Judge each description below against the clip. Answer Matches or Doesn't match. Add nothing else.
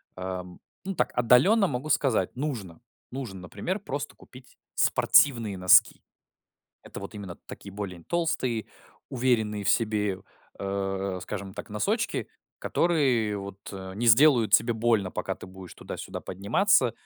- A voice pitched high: Doesn't match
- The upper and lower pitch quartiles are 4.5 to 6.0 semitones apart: Matches